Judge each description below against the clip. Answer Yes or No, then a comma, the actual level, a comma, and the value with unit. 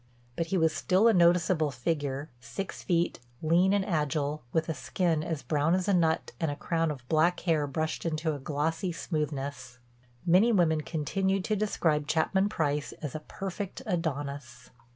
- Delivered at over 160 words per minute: Yes, average, 170 wpm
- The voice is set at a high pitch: No, medium, 160 Hz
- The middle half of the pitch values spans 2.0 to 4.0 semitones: Yes, average, 3.3 semitones